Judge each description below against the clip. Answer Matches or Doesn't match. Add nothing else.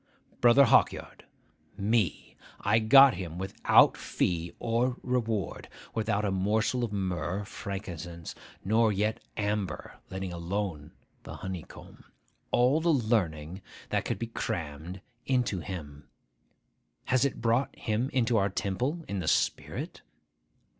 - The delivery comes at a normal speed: Doesn't match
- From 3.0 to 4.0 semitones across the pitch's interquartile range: Doesn't match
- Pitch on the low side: Matches